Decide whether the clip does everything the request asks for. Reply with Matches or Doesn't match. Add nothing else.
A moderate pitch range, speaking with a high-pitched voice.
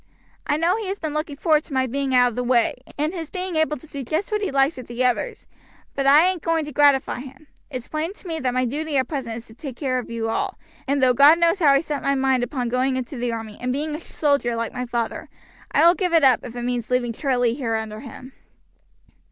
Matches